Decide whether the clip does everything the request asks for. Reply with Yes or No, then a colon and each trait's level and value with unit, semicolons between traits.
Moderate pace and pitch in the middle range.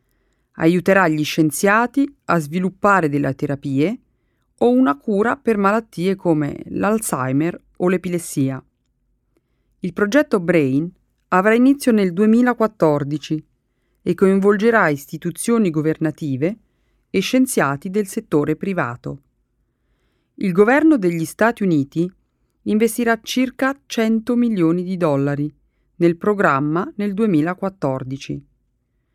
No: slow, 95 wpm; medium, 180 Hz